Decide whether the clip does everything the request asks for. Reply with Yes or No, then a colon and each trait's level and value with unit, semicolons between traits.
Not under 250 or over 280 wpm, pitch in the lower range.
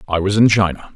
Yes: fast, 255 wpm; low, 100 Hz